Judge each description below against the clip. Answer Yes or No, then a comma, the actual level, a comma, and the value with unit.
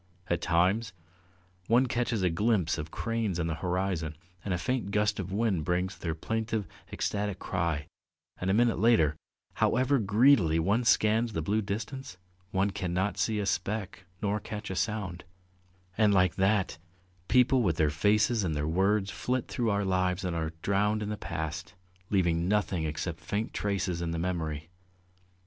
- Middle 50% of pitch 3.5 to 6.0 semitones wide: Yes, average, 3.9 semitones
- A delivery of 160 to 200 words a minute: Yes, average, 165 wpm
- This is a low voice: Yes, very low, 95 Hz